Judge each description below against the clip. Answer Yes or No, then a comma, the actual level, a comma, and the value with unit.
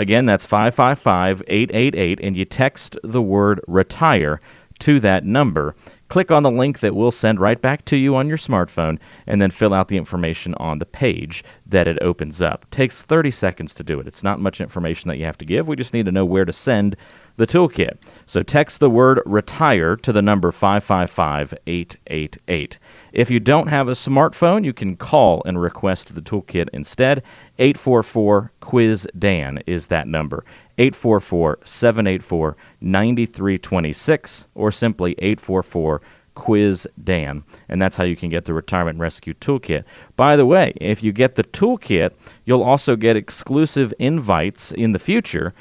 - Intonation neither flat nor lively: No, wide, 5.8 semitones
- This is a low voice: Yes, low, 100 Hz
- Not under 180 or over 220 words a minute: No, average, 165 wpm